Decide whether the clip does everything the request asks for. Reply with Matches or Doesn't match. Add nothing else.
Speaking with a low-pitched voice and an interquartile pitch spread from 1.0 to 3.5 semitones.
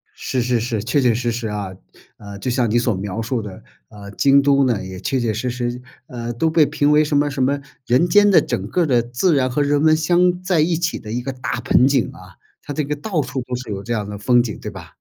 Doesn't match